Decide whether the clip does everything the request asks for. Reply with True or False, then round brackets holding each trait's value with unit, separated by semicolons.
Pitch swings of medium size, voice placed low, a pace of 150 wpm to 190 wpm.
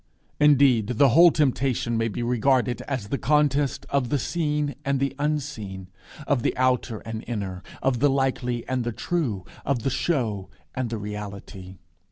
True (4.0 semitones; 125 Hz; 165 wpm)